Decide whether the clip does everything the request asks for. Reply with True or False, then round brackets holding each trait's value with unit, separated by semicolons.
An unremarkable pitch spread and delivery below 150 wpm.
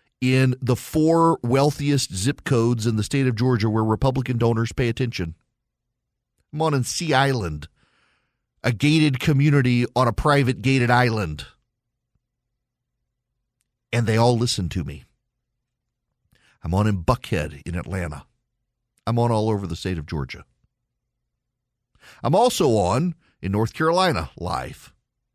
True (3.6 semitones; 135 wpm)